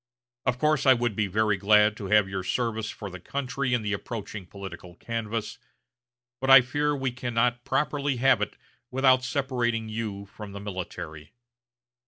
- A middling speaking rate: Yes, average, 165 wpm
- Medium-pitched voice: No, low, 115 Hz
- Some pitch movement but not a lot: Yes, average, 3.8 semitones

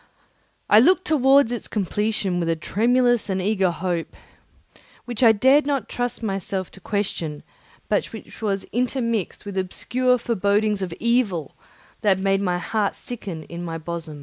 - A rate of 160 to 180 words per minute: No, average, 140 wpm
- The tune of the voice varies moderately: Yes, average, 4.3 semitones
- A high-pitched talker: Yes, high, 210 Hz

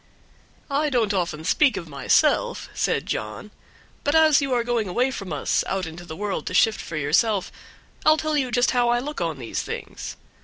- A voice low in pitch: No, high, 210 Hz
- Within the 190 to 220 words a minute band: Yes, average, 195 wpm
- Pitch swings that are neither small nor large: No, wide, 7.8 semitones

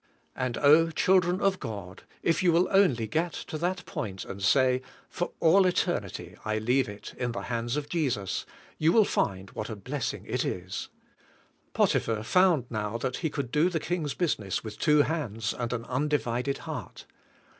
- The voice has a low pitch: Yes, low, 130 Hz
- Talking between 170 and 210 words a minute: Yes, average, 180 wpm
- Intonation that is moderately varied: No, wide, 7.2 semitones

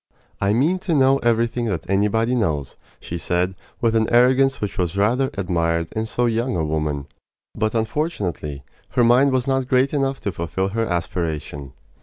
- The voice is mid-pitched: No, low, 110 Hz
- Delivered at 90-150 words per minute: No, average, 170 wpm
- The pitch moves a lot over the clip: Yes, wide, 6.5 semitones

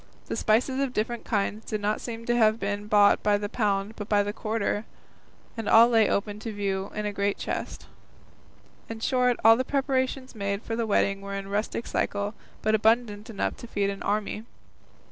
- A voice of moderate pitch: No, high, 215 Hz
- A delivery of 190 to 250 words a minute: Yes, average, 195 wpm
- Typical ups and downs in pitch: No, narrow, 2.1 semitones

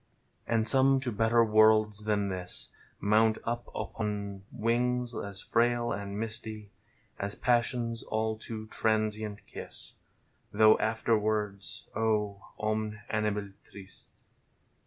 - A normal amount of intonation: No, narrow, 1.6 semitones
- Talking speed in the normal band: No, slow, 115 wpm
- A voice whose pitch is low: Yes, low, 110 Hz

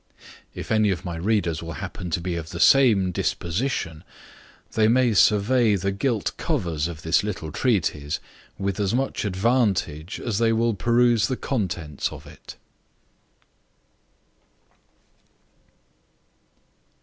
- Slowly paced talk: Yes, slow, 120 wpm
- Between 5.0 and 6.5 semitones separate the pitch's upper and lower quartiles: Yes, average, 5.3 semitones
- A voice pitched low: Yes, low, 100 Hz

